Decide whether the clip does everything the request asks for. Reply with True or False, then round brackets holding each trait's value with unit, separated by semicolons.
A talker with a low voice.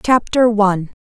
False (215 Hz)